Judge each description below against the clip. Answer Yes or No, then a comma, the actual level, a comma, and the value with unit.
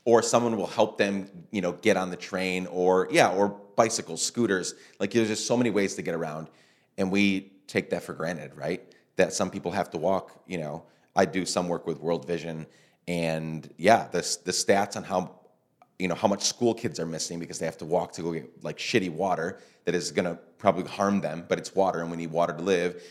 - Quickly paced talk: Yes, fast, 230 wpm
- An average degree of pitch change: Yes, average, 3.1 semitones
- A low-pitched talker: Yes, very low, 90 Hz